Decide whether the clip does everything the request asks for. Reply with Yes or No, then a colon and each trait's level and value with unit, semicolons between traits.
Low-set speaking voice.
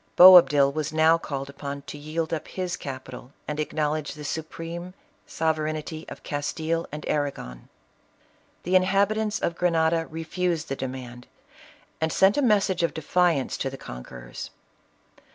No: medium, 155 Hz